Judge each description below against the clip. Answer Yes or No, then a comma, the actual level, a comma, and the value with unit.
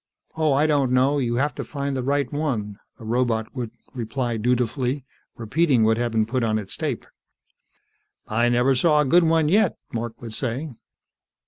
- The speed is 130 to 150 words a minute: No, average, 180 wpm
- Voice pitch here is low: Yes, low, 125 Hz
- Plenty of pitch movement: No, average, 3.9 semitones